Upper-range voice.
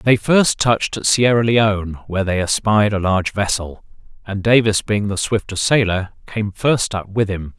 No: low, 105 Hz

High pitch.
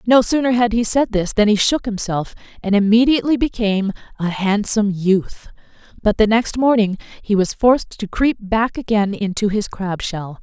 Yes: high, 215 Hz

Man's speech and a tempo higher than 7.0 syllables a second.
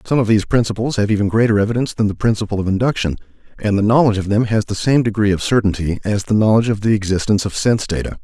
Yes: male; 7.5 syllables/s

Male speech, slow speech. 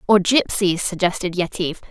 No: female; slow, 125 wpm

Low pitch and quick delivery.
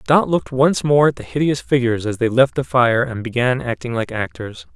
Yes: low, 125 Hz; fast, 225 wpm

